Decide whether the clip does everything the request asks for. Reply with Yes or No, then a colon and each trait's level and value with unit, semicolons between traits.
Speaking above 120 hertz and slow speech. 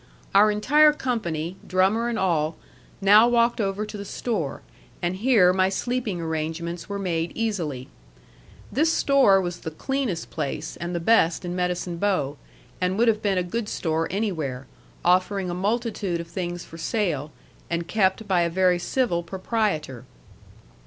No: medium, 185 Hz; average, 155 wpm